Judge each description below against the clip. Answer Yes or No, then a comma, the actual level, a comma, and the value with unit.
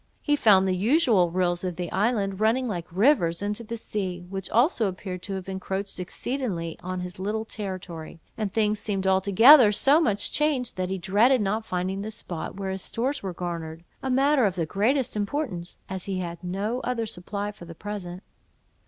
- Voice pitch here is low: No, high, 195 Hz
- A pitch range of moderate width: Yes, average, 3.8 semitones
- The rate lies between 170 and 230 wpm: Yes, average, 190 wpm